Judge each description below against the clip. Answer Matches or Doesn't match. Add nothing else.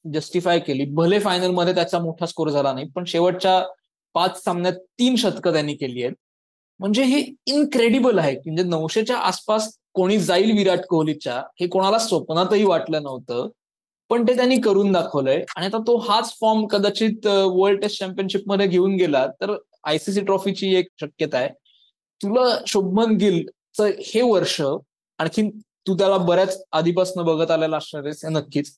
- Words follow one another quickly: Matches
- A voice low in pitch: Doesn't match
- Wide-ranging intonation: Doesn't match